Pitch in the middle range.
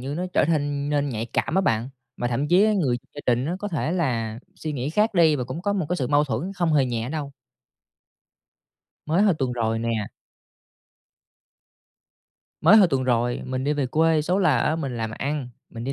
Yes: medium, 145 Hz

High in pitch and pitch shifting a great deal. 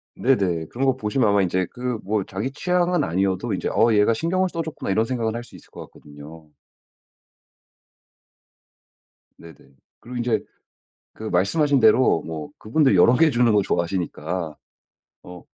No: low, 110 Hz; wide, 6.1 semitones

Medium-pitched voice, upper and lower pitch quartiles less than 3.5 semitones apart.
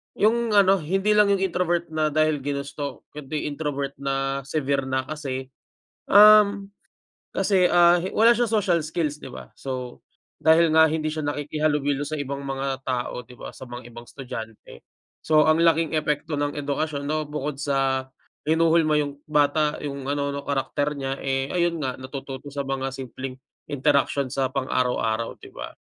Yes: medium, 145 Hz; average, 2.8 semitones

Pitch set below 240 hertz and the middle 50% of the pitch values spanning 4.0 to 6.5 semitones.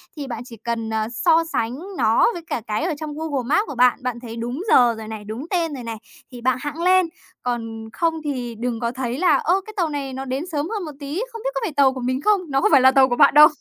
No: very high, 265 Hz; average, 5.2 semitones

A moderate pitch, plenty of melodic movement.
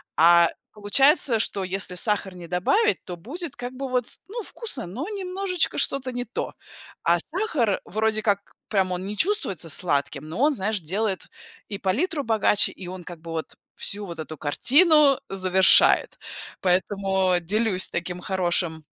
No: high, 200 Hz; wide, 6.9 semitones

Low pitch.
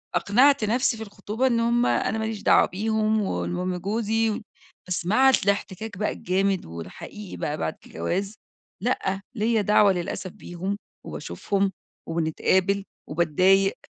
No: high, 200 Hz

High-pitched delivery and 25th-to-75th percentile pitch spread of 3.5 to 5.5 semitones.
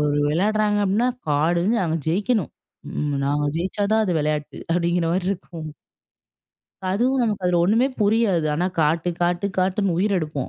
No: medium, 180 Hz; average, 4.1 semitones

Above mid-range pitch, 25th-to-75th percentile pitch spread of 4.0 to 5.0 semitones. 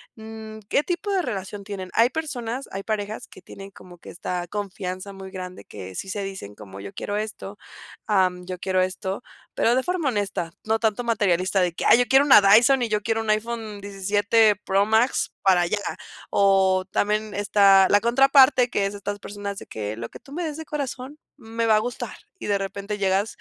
No: high, 205 Hz; average, 3.3 semitones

